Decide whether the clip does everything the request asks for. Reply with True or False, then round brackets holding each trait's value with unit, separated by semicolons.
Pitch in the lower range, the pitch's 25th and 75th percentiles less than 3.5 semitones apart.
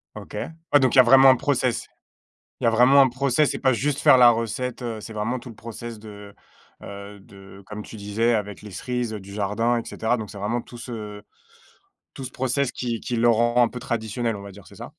True (115 Hz; 3.0 semitones)